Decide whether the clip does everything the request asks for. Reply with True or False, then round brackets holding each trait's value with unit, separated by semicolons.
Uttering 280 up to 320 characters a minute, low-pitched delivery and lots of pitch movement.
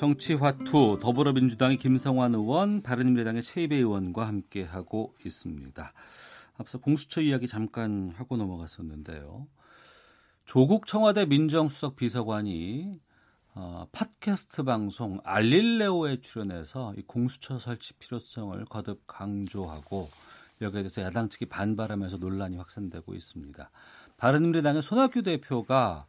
True (315 characters per minute; 120 Hz; 6.1 semitones)